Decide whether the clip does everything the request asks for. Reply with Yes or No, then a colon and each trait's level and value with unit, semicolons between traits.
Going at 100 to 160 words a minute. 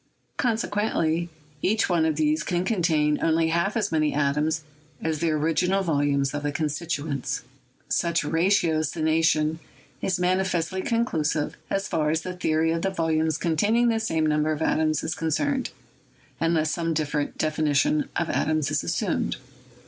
Yes: average, 150 wpm